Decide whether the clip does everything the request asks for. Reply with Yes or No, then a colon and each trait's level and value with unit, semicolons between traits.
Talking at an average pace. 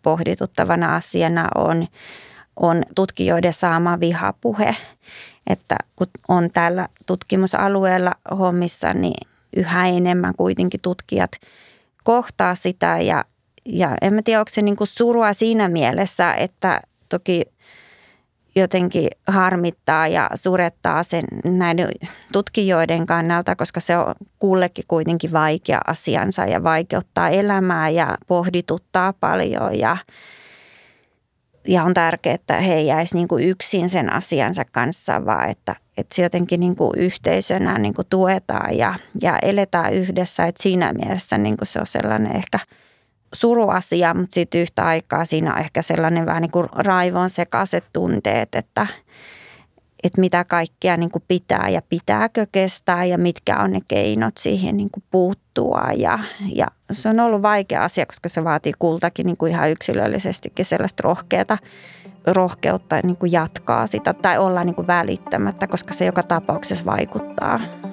Yes: average, 135 wpm